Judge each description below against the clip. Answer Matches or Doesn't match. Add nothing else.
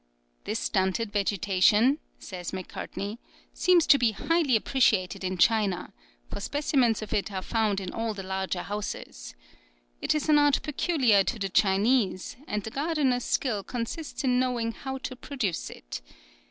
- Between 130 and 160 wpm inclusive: Matches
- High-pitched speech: Matches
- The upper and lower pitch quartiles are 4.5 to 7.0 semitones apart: Matches